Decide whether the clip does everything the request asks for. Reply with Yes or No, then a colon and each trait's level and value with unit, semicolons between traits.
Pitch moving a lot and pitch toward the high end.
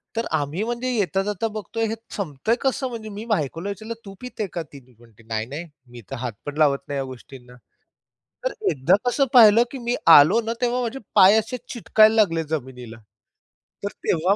Yes: wide, 8.4 semitones; high, 195 Hz